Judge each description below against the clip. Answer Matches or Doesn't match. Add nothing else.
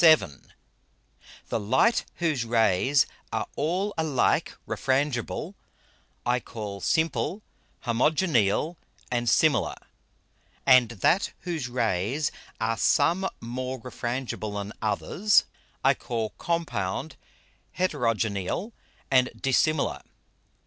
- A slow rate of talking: Matches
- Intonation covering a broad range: Matches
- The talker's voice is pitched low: Matches